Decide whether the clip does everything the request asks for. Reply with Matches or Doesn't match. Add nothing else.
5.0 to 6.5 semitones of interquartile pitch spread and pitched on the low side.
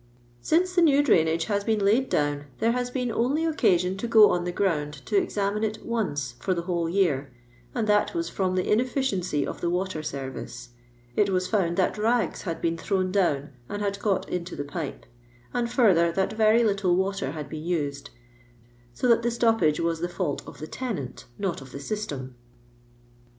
Doesn't match